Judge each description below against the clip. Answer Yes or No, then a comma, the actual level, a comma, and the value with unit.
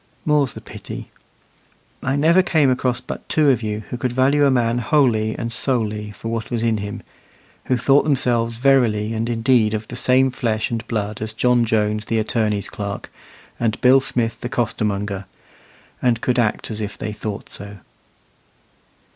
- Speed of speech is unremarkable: Yes, average, 170 wpm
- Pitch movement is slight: No, average, 3.0 semitones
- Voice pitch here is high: No, low, 115 Hz